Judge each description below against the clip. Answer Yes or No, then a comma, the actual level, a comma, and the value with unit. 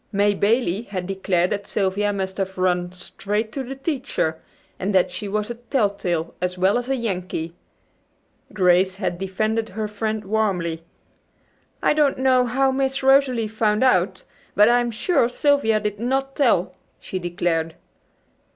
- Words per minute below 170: Yes, average, 150 wpm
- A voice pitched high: Yes, high, 210 Hz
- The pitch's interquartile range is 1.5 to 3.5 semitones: No, average, 4.6 semitones